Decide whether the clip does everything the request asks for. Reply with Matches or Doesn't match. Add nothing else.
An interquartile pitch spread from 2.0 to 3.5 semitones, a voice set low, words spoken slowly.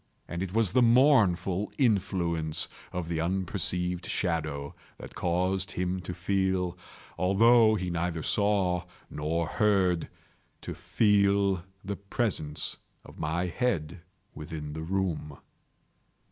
Matches